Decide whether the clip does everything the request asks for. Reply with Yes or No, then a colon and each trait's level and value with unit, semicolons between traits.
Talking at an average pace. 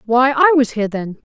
No: fast, 230 wpm